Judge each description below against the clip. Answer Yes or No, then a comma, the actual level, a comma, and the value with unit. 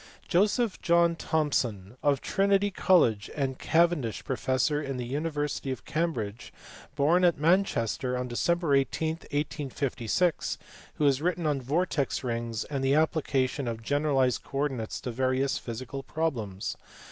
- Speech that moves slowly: Yes, slow, 130 wpm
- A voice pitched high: No, medium, 140 Hz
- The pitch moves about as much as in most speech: Yes, average, 4.4 semitones